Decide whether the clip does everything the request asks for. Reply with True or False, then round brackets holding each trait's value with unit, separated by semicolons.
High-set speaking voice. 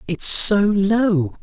True (195 Hz)